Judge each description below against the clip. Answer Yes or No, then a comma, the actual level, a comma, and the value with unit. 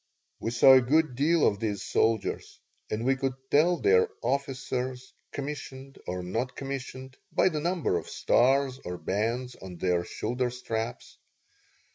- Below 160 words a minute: Yes, average, 145 wpm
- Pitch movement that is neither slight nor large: Yes, average, 3.7 semitones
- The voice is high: No, low, 130 Hz